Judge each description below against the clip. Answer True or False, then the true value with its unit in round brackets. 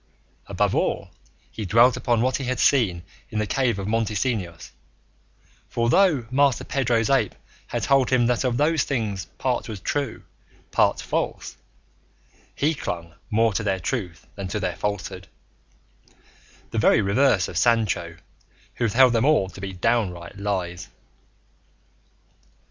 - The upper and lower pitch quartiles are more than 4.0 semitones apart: True (5.0 semitones)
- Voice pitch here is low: True (115 Hz)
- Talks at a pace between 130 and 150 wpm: True (145 wpm)